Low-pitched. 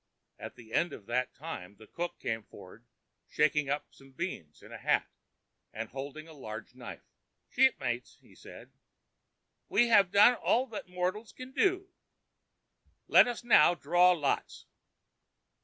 No: medium, 160 Hz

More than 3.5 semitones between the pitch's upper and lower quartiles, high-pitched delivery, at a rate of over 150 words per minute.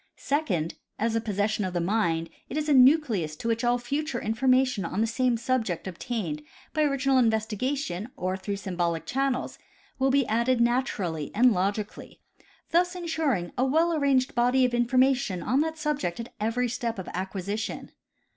Yes: average, 5.2 semitones; high, 235 Hz; average, 170 wpm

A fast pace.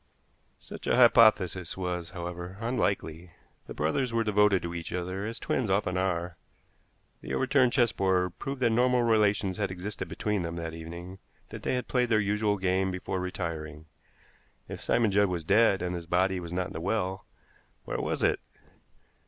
No: average, 170 wpm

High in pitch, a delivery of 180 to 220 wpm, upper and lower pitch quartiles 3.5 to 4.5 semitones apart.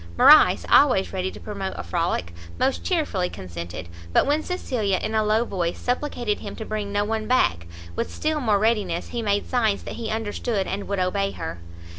Yes: high, 210 Hz; average, 190 wpm; average, 4.0 semitones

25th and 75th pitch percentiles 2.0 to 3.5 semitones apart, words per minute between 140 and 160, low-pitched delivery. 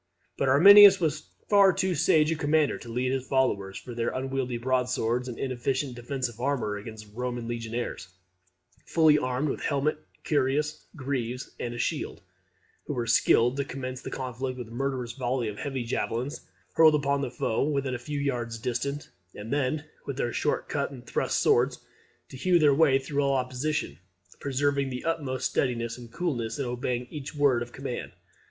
No: average, 2.9 semitones; average, 175 wpm; low, 130 Hz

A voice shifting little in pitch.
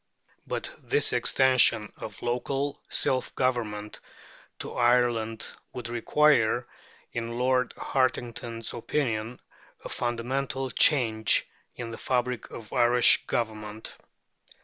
Yes: narrow, 2.1 semitones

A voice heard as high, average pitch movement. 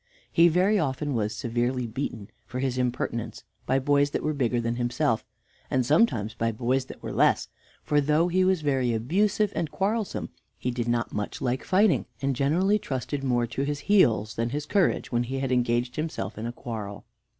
No: low, 130 Hz; average, 4.3 semitones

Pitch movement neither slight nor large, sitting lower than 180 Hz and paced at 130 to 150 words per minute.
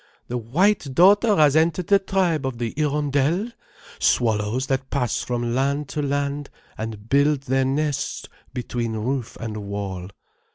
Yes: average, 4.3 semitones; low, 135 Hz; average, 140 wpm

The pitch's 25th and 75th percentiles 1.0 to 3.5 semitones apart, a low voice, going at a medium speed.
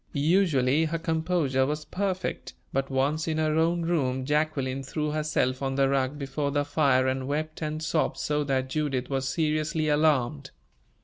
No: average, 2.7 semitones; medium, 150 Hz; average, 165 wpm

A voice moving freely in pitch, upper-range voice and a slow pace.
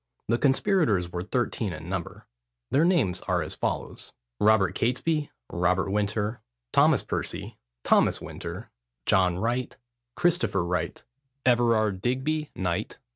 No: wide, 5.7 semitones; low, 110 Hz; slow, 120 wpm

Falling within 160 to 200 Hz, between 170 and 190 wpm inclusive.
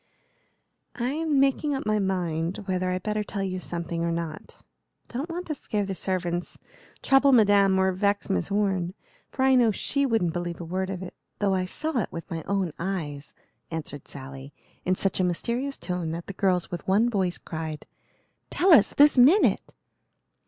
Yes: high, 190 Hz; average, 180 wpm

